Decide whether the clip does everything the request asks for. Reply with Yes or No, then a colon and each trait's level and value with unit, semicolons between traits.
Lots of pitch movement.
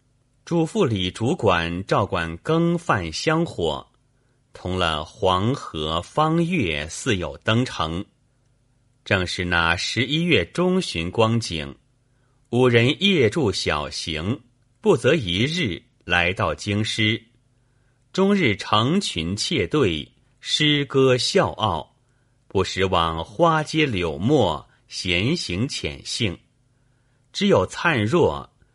Yes: wide, 6.4 semitones